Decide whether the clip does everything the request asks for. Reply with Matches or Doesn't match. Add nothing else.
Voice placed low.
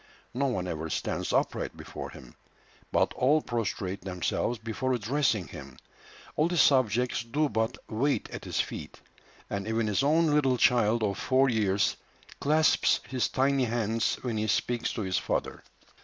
Matches